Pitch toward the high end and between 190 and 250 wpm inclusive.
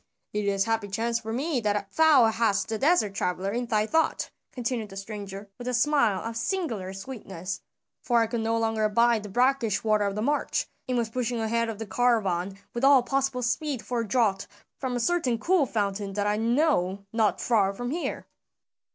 Yes: high, 225 Hz; average, 200 wpm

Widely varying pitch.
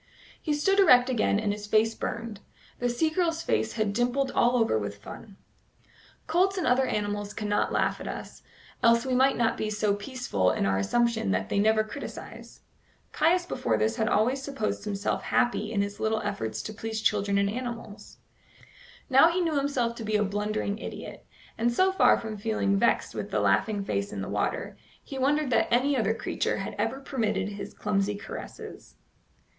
No: average, 3.9 semitones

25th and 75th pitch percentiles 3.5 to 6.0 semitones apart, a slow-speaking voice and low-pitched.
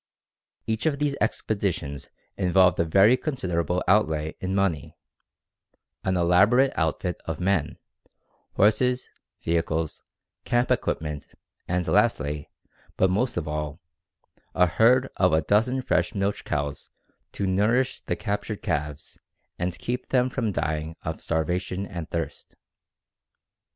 Yes: average, 5.2 semitones; slow, 125 wpm; very low, 90 Hz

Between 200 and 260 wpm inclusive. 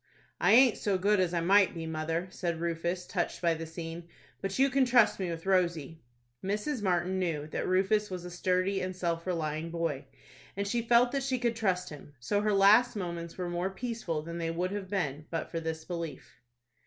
Yes: fast, 205 wpm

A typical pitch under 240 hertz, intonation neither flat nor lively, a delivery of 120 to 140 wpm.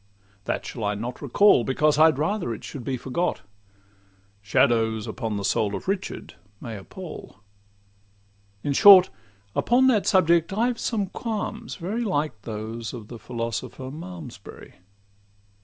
No: low, 135 Hz; wide, 8.7 semitones; slow, 135 wpm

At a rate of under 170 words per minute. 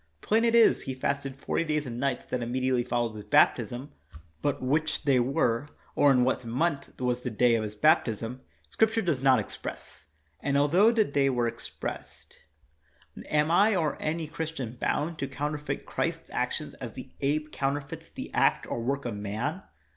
No: average, 185 wpm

